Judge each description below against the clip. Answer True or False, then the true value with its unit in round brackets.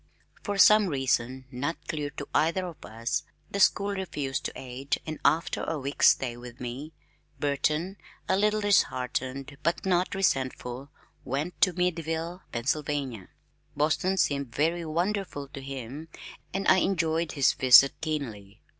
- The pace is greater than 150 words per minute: False (140 wpm)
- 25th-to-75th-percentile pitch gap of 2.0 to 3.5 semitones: False (5.0 semitones)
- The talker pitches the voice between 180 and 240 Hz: False (150 Hz)